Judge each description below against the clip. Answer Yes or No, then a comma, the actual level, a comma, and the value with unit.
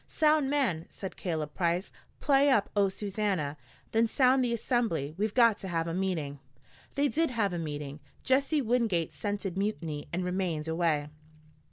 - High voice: Yes, high, 195 Hz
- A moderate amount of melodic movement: No, wide, 6.6 semitones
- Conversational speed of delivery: Yes, average, 160 wpm